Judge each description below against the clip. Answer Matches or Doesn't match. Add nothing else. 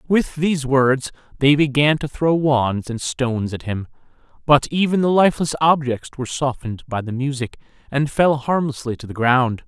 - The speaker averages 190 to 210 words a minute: Doesn't match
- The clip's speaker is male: Matches